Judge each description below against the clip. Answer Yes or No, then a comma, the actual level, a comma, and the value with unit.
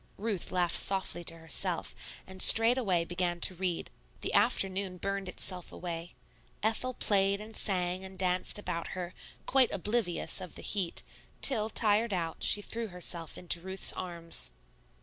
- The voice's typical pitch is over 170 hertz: Yes, medium, 185 Hz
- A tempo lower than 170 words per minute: Yes, average, 150 wpm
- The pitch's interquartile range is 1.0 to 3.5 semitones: Yes, average, 2.9 semitones